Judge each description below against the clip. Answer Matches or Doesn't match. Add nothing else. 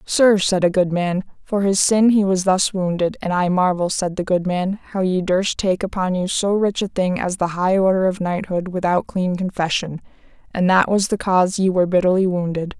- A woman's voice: Matches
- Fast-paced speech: Matches